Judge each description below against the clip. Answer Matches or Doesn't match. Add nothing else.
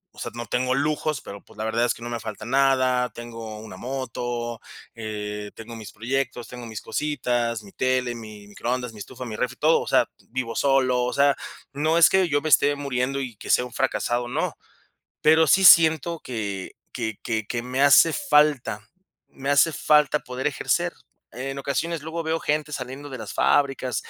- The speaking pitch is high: Doesn't match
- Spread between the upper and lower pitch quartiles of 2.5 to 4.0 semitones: Matches